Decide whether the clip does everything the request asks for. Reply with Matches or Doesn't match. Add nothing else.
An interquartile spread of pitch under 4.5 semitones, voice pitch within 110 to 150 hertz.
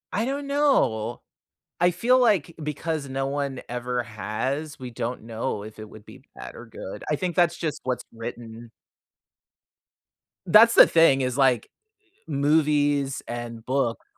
Doesn't match